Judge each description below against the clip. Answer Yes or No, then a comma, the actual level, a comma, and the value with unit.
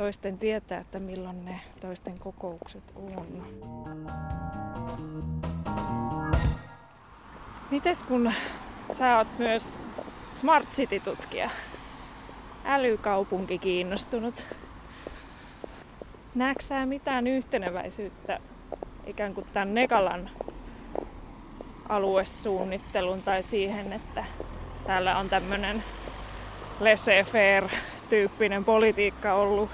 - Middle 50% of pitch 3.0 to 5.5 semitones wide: Yes, average, 3.5 semitones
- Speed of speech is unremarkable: No, slow, 70 wpm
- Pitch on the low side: No, high, 195 Hz